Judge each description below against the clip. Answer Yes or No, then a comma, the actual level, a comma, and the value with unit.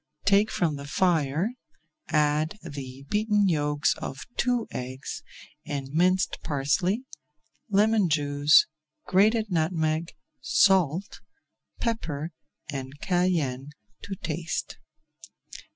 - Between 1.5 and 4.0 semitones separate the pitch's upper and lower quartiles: No, average, 5.1 semitones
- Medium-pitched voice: Yes, medium, 160 Hz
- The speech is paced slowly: Yes, slow, 90 wpm